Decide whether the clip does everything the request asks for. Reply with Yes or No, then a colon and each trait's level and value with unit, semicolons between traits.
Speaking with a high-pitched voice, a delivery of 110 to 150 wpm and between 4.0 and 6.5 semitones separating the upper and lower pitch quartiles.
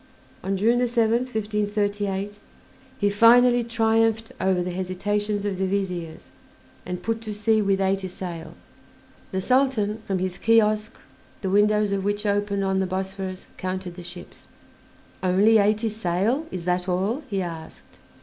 No: high, 205 Hz; average, 145 wpm; average, 2.7 semitones